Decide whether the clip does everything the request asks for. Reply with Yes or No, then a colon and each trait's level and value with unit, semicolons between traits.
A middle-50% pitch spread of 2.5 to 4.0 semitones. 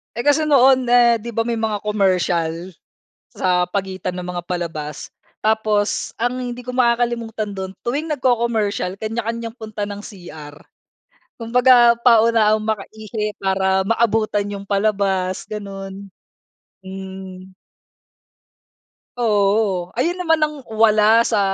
Yes: average, 3.5 semitones